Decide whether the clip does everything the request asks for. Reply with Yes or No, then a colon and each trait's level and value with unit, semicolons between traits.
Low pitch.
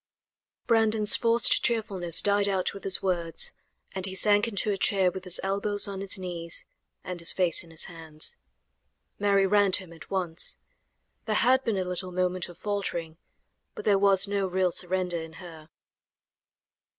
No: high, 190 Hz